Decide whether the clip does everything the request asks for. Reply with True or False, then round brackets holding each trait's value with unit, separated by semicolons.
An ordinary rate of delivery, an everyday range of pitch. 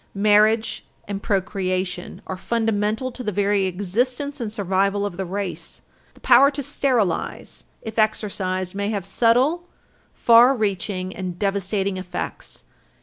False (130 wpm; 3.4 semitones)